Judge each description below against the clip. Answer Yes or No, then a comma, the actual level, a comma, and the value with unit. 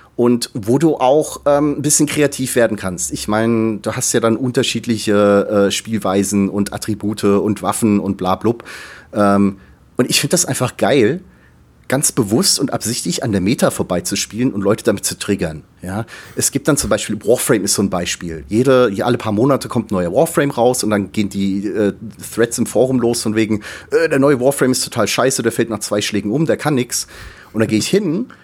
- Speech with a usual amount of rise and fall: Yes, average, 3.9 semitones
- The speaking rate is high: Yes, fast, 205 wpm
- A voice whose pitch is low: Yes, low, 110 Hz